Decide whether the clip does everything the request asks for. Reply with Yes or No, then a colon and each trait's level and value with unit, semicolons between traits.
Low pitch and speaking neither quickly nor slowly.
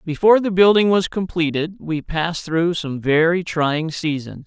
No: medium, 170 Hz; average, 160 wpm